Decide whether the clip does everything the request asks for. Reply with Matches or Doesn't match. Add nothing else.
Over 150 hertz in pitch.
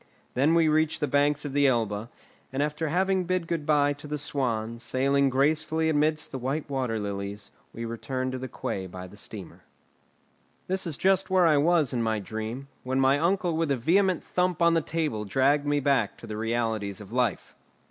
Doesn't match